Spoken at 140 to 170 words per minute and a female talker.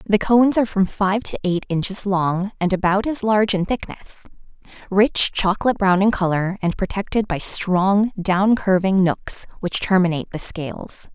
Yes: average, 165 wpm; female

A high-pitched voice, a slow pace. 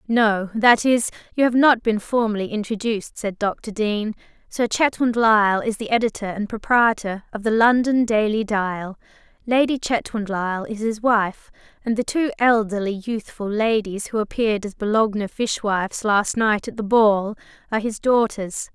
No: high, 220 Hz; average, 155 wpm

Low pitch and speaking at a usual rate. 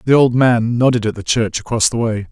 No: low, 115 Hz; fast, 260 wpm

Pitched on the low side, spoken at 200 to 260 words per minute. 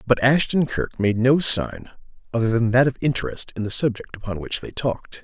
Yes: low, 120 Hz; fast, 205 wpm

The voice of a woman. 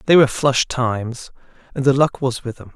No: male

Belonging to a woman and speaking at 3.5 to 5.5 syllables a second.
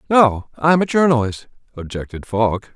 No: male; 4.6 syllables/s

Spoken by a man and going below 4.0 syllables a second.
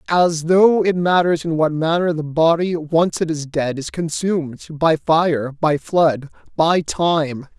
Yes: male; 3.7 syllables/s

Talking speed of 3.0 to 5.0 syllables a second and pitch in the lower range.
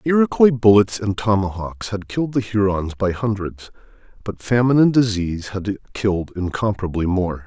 No: 5.2 syllables/s; low, 105 Hz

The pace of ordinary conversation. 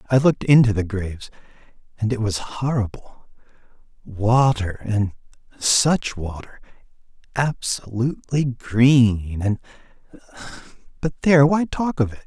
No: slow, 105 wpm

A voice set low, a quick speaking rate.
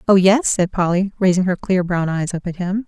No: medium, 185 Hz; fast, 250 wpm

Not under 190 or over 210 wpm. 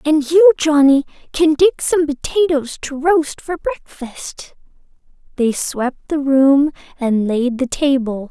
No: slow, 135 wpm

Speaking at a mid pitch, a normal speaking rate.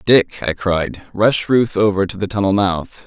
No: low, 100 Hz; average, 195 wpm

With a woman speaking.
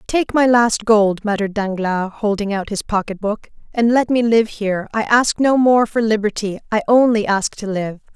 Yes: female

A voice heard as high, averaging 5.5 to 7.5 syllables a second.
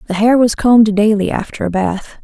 Yes: high, 215 Hz; 5.6 syllables/s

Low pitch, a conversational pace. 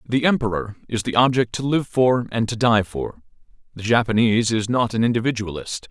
Yes: low, 115 Hz; average, 185 wpm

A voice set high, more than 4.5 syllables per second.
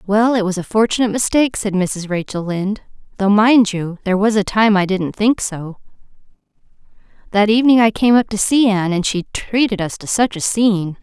Yes: high, 205 Hz; 5.7 syllables/s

